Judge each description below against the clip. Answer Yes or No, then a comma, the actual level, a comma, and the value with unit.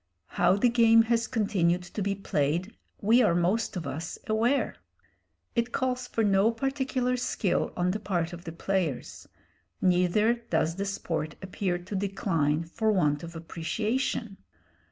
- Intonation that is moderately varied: Yes, average, 4.8 semitones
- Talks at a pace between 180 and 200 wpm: No, average, 150 wpm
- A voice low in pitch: No, high, 195 Hz